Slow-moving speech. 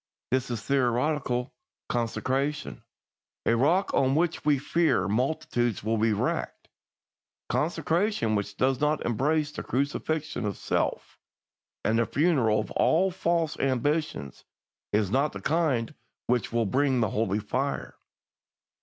Yes: slow, 125 wpm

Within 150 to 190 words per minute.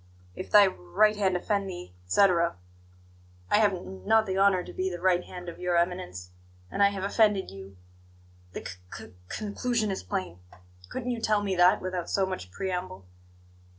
Yes: average, 185 wpm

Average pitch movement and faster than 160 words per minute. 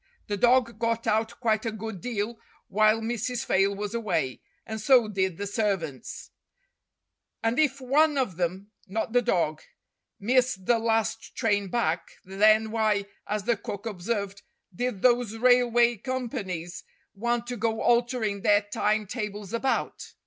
No: average, 3.0 semitones; average, 145 wpm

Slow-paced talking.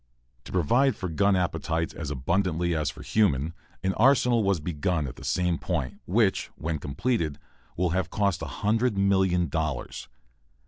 No: average, 155 wpm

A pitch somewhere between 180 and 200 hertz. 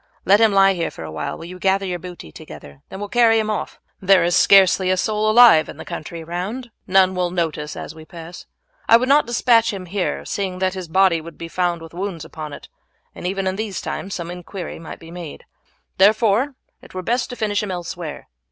Yes: medium, 185 Hz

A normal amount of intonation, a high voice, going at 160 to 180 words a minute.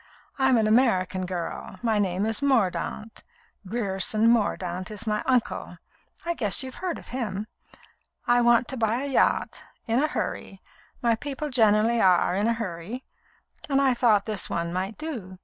Yes: average, 4.6 semitones; high, 225 Hz; average, 165 wpm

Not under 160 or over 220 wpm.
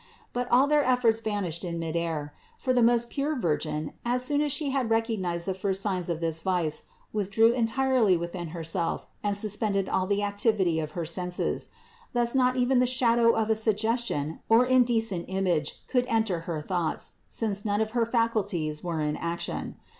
Yes: average, 175 wpm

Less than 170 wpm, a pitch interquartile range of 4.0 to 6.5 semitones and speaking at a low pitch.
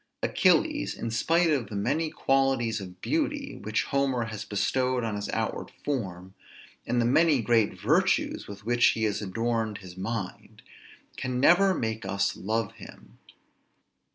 Yes: average, 150 wpm; average, 4.7 semitones; low, 115 Hz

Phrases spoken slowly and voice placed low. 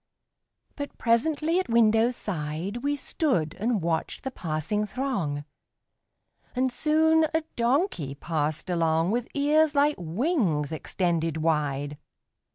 No: slow, 115 wpm; high, 215 Hz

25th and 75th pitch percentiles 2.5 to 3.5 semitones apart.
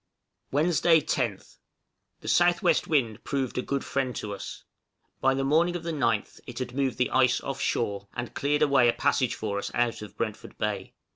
No: average, 4.0 semitones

